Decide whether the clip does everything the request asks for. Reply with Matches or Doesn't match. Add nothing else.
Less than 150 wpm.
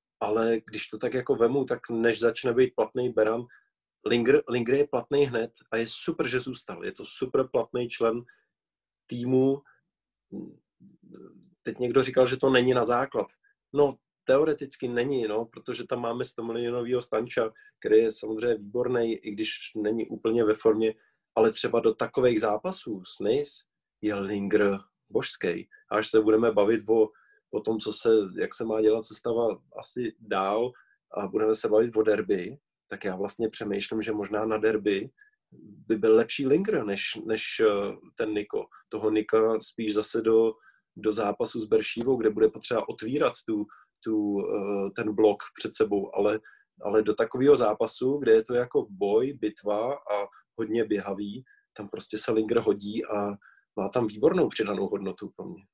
Doesn't match